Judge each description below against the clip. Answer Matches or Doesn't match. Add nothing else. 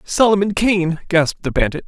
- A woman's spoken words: Doesn't match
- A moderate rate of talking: Matches